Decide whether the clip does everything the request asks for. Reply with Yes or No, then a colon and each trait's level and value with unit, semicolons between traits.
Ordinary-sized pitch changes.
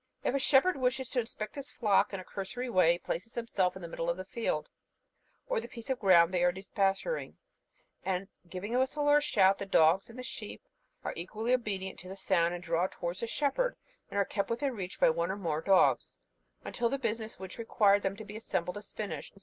Yes: average, 4.7 semitones